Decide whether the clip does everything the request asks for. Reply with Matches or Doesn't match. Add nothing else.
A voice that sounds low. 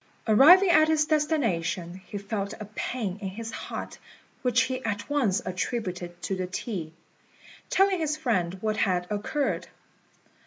Doesn't match